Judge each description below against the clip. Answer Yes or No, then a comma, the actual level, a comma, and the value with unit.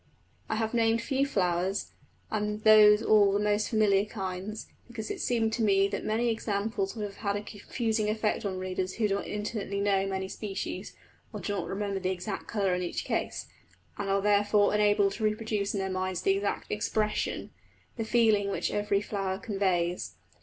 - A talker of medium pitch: No, high, 205 Hz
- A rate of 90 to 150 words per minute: No, average, 185 wpm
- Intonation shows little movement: Yes, narrow, 1.8 semitones